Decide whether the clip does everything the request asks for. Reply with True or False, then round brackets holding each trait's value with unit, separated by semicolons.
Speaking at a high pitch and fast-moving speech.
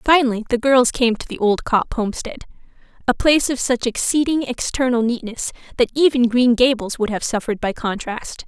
False (240 Hz; 175 wpm)